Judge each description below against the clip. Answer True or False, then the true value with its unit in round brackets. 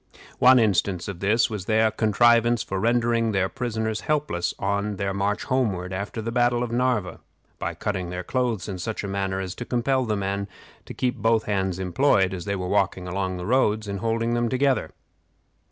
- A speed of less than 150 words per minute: False (185 wpm)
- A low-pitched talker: True (105 Hz)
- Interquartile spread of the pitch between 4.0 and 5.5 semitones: False (3.6 semitones)